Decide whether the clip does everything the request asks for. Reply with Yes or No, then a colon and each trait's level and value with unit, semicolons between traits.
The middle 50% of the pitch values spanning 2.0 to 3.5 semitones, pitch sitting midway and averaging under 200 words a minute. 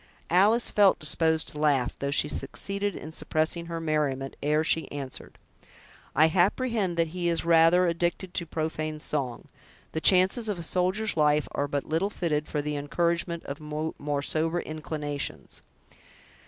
Yes: average, 2.7 semitones; medium, 160 Hz; average, 155 wpm